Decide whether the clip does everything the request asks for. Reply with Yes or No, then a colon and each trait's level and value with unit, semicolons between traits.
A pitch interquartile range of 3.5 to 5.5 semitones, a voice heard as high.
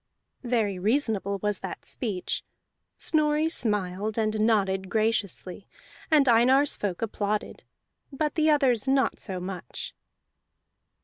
Yes: average, 5.1 semitones; high, 220 Hz